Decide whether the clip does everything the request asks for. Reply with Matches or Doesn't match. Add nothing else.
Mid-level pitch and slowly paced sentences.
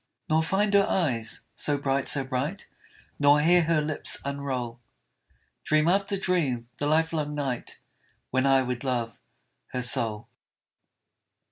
Matches